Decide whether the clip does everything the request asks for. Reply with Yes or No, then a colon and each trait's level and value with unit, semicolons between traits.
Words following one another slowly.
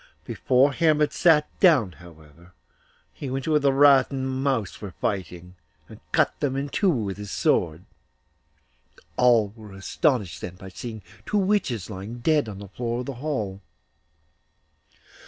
No: average, 155 wpm